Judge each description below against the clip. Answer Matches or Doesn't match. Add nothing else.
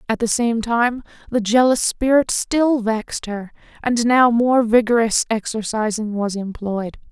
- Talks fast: Doesn't match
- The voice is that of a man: Doesn't match